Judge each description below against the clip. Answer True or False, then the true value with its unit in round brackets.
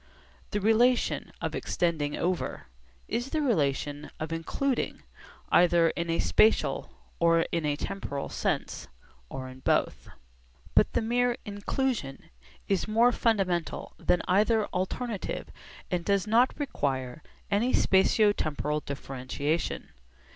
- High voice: False (180 Hz)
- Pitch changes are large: True (6.8 semitones)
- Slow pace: True (120 wpm)